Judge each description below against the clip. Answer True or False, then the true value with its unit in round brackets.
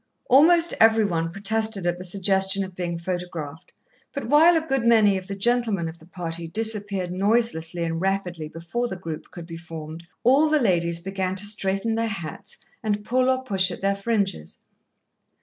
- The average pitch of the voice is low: False (195 Hz)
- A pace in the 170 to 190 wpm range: True (180 wpm)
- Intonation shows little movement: False (4.6 semitones)